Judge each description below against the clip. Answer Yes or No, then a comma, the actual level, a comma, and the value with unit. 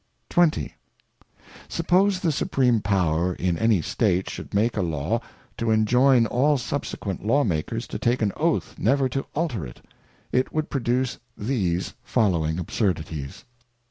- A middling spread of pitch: No, wide, 6.6 semitones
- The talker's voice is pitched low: Yes, low, 115 Hz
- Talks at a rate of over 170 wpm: No, average, 140 wpm